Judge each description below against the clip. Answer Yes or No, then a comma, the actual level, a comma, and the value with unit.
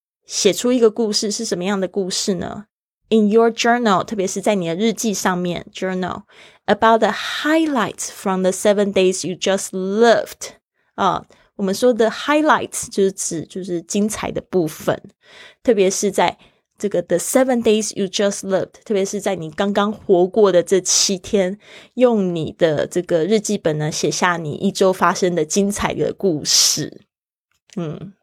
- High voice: Yes, high, 200 Hz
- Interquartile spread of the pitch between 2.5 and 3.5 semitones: Yes, average, 3.2 semitones